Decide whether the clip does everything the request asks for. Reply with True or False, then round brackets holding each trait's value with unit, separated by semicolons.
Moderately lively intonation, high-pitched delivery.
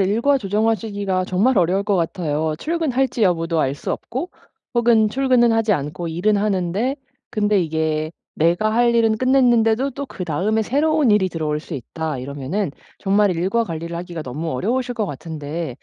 False (5.9 semitones; 195 Hz)